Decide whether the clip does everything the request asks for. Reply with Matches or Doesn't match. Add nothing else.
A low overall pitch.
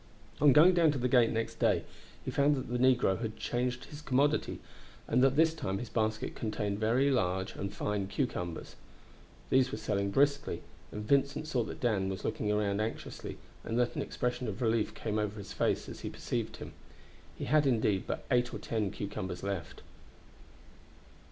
Matches